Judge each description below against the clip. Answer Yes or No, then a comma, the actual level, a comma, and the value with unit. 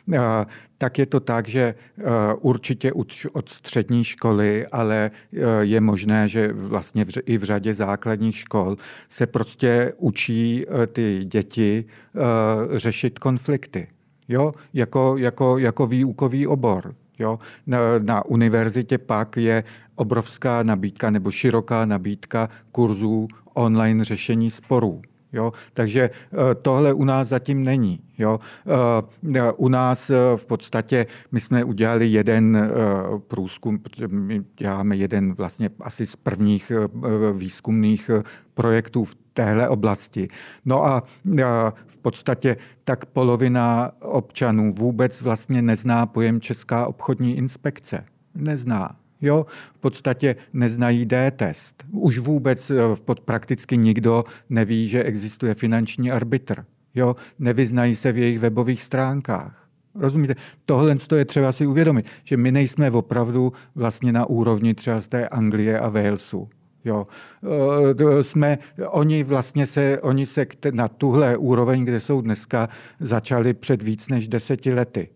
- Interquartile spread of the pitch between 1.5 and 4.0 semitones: Yes, average, 2.9 semitones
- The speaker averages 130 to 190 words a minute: No, average, 120 wpm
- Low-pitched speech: Yes, low, 120 Hz